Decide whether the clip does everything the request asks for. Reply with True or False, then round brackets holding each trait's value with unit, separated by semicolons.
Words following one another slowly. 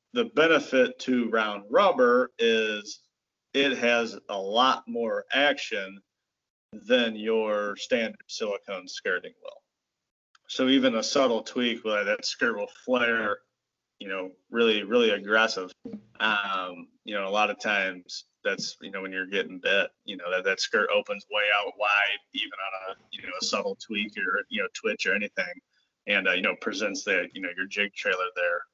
False (170 wpm)